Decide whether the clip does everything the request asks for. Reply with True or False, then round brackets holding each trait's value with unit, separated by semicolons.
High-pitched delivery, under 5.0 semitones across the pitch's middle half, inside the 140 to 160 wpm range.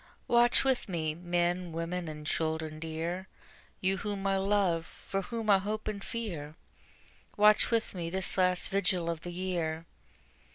False (180 Hz; 3.2 semitones; 155 wpm)